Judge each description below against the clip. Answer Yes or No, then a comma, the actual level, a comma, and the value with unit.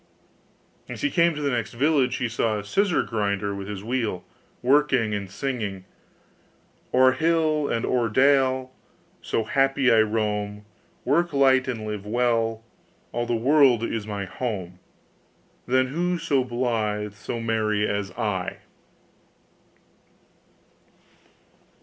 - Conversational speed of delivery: No, slow, 125 wpm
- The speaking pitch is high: No, low, 120 Hz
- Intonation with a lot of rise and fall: No, average, 4.3 semitones